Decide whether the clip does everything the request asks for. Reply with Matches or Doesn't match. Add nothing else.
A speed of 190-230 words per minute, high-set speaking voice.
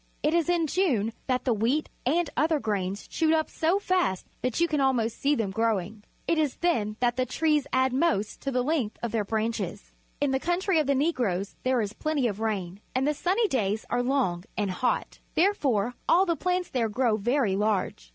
Matches